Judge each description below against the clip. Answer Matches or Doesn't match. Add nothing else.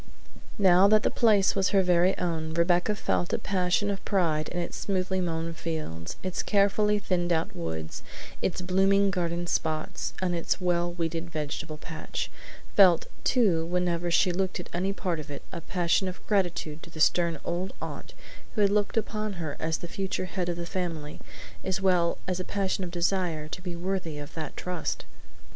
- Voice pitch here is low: Doesn't match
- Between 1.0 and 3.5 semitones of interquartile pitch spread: Matches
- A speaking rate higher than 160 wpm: Matches